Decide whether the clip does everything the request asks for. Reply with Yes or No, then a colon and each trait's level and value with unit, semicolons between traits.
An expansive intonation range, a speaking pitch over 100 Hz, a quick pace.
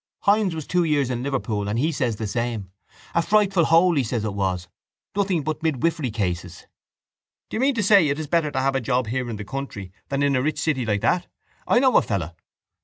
Yes: wide, 7.2 semitones; low, 135 Hz; fast, 230 wpm